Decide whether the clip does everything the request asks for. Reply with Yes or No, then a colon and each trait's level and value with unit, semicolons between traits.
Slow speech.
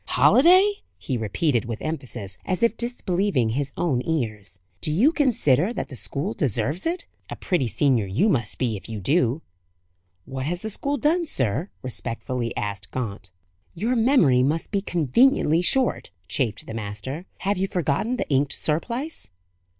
No: average, 160 wpm